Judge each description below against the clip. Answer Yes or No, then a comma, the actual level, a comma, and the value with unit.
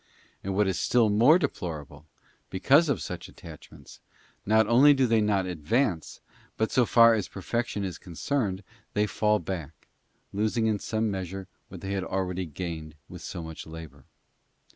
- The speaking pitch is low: Yes, low, 100 Hz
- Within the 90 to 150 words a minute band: No, average, 165 wpm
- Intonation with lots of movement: No, average, 4.0 semitones